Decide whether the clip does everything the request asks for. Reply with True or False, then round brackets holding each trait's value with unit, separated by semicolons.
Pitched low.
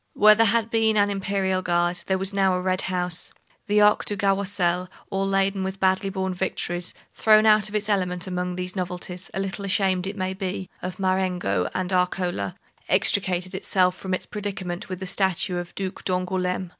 False (190 Hz)